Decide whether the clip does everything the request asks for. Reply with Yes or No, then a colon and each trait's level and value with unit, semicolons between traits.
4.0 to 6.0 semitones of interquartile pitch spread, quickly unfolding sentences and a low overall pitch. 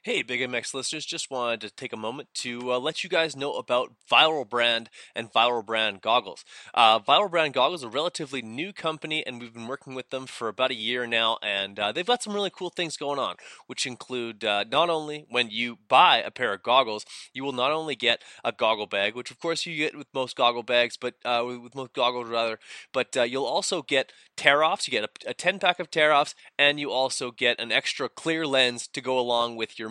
Yes: average, 4.3 semitones; fast, 230 wpm; low, 125 Hz